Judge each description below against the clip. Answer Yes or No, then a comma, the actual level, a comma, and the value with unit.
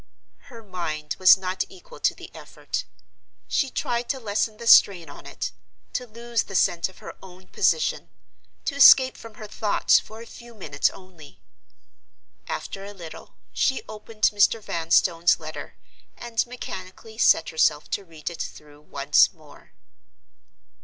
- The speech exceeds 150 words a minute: No, average, 145 wpm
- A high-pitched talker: Yes, high, 195 Hz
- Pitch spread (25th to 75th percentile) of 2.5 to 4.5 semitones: No, wide, 5.6 semitones